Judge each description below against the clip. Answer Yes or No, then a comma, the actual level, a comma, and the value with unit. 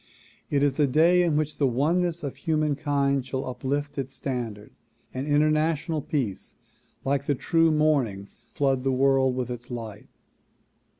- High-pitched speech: No, medium, 140 Hz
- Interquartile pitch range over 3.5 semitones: No, average, 3.0 semitones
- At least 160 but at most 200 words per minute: No, average, 145 wpm